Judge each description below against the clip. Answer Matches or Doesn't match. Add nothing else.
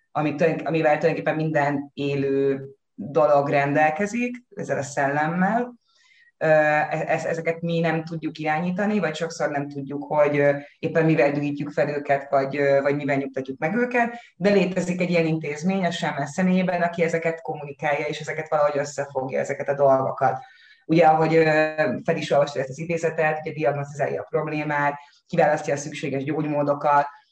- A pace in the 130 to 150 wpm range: Matches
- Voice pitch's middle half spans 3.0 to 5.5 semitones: Doesn't match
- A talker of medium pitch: Matches